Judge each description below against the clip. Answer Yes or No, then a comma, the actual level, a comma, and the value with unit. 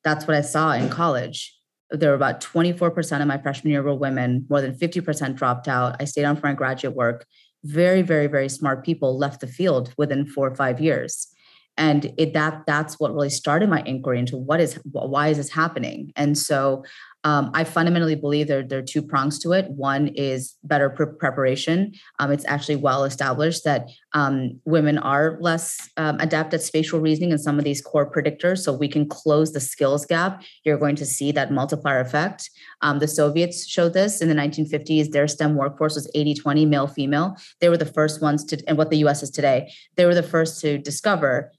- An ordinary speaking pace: No, fast, 210 wpm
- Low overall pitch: No, medium, 150 Hz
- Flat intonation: Yes, narrow, 2.1 semitones